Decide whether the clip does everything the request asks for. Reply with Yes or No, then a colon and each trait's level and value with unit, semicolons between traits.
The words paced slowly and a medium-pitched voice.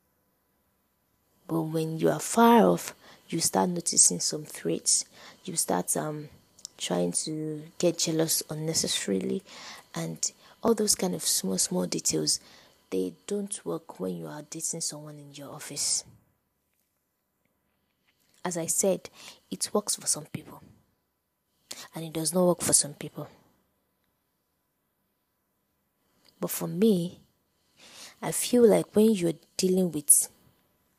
Yes: slow, 125 wpm; medium, 150 Hz